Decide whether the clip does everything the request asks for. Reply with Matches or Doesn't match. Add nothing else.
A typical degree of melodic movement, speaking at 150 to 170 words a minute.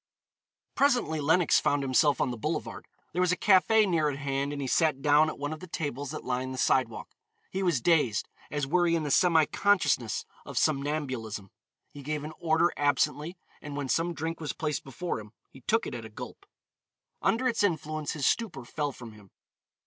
Doesn't match